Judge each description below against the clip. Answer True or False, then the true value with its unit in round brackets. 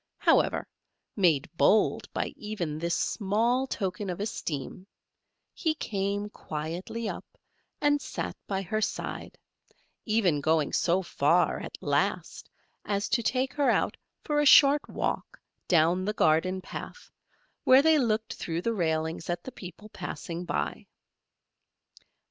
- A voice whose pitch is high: True (195 Hz)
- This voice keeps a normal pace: False (130 wpm)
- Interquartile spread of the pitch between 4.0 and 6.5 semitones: True (5.1 semitones)